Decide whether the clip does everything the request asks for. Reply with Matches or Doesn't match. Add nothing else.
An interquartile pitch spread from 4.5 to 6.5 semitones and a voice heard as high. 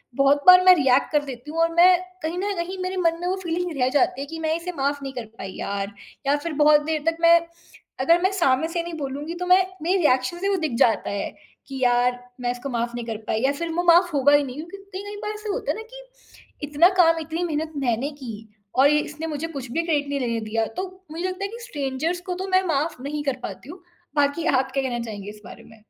Matches